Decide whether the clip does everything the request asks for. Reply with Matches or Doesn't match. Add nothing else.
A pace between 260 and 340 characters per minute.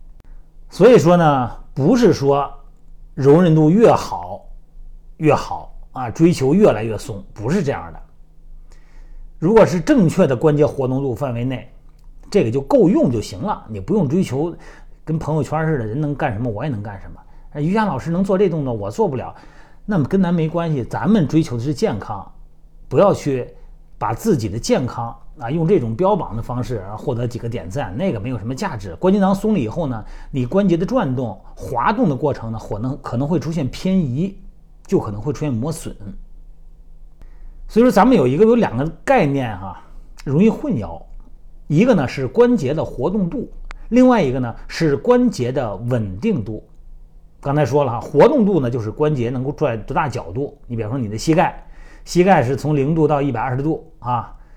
Matches